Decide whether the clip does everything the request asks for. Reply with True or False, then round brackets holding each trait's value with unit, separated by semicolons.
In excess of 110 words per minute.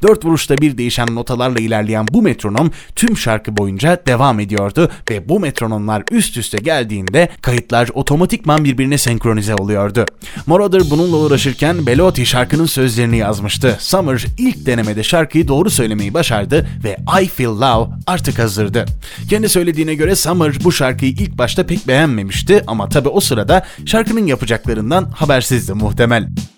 True (140 wpm)